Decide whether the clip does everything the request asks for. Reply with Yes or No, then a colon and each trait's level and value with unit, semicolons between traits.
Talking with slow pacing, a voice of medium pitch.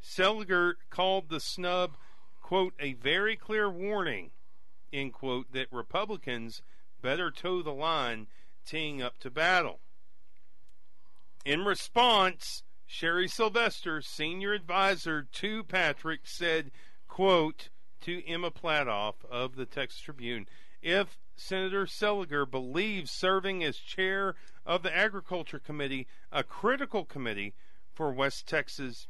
Yes: slow, 115 wpm; medium, 170 Hz